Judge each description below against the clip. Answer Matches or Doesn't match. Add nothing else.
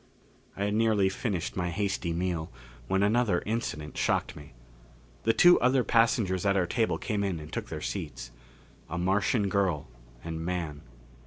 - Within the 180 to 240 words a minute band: Doesn't match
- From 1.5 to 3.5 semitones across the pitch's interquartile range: Doesn't match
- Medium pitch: Doesn't match